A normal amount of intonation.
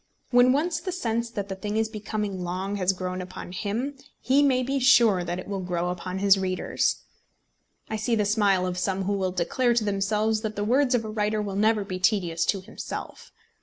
Yes: average, 3.6 semitones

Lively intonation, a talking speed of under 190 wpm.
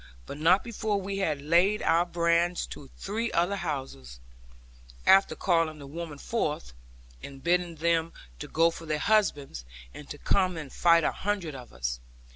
No: average, 4.1 semitones; average, 160 wpm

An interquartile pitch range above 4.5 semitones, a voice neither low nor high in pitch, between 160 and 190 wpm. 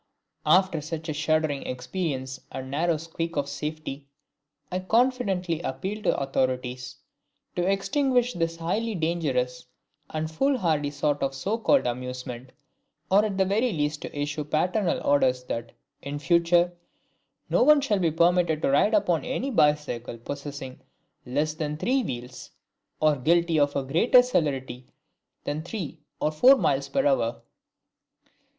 No: average, 5.2 semitones; medium, 155 Hz; average, 145 wpm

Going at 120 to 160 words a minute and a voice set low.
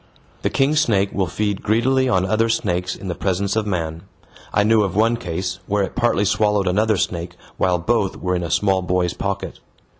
No: average, 200 wpm; low, 100 Hz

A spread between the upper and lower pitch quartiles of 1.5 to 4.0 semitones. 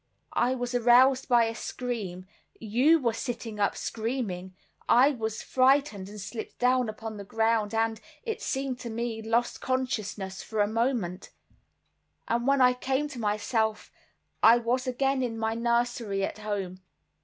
Yes: average, 2.8 semitones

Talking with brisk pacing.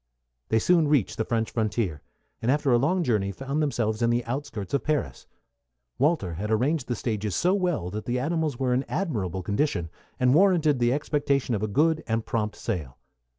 No: average, 190 wpm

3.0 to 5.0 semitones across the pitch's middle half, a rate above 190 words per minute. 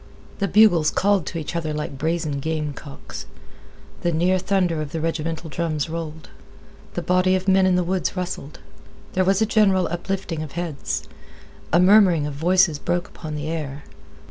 No: average, 3.3 semitones; average, 170 wpm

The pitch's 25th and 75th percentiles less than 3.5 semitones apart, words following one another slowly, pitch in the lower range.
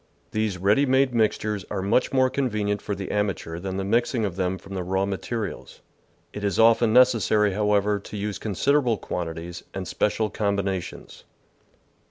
No: average, 2.7 semitones; average, 165 wpm; low, 105 Hz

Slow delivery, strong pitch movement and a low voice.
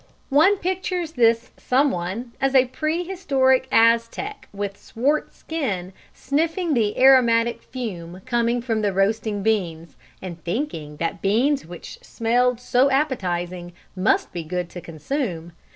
No: slow, 125 wpm; wide, 6.6 semitones; high, 230 Hz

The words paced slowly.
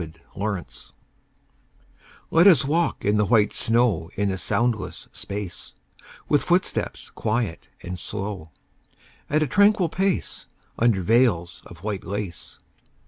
Yes: slow, 125 wpm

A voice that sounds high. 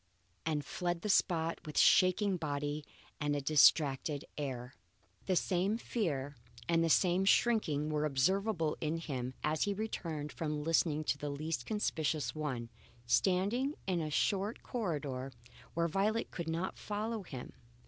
No: medium, 160 Hz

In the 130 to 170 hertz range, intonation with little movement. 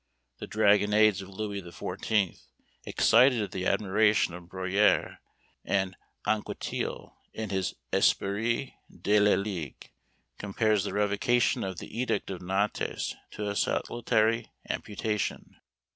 No: low, 105 Hz; narrow, 2.1 semitones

